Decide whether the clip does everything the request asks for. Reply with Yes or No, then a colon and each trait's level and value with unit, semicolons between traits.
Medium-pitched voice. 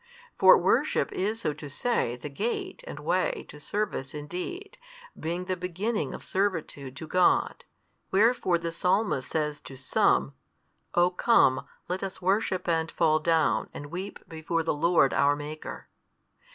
Yes: medium, 170 Hz